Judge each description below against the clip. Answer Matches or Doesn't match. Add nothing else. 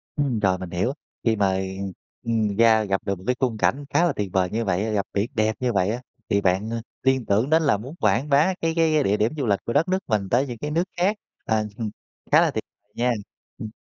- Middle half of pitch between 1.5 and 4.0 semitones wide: Doesn't match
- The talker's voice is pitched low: Matches